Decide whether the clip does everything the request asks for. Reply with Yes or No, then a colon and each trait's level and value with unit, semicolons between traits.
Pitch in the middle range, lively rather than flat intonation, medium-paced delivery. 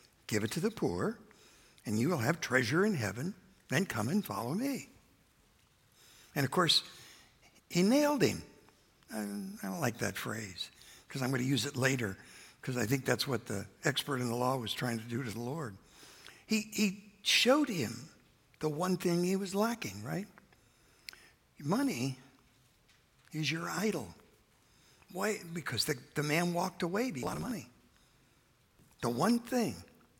Yes: medium, 150 Hz; wide, 8.2 semitones; average, 165 wpm